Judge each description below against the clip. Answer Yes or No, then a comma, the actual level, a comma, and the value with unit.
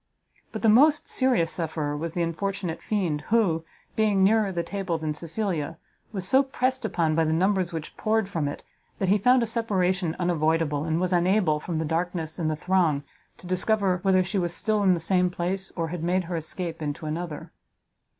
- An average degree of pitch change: Yes, average, 3.6 semitones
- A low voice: No, medium, 180 Hz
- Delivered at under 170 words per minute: No, average, 195 wpm